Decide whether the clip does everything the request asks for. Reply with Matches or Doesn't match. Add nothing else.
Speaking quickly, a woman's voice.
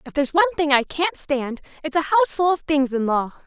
Matches